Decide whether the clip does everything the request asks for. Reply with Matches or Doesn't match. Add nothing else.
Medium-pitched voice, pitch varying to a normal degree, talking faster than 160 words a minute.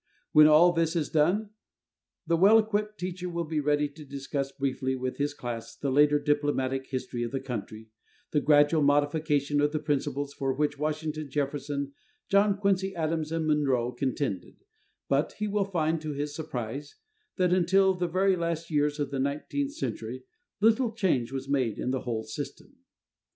Matches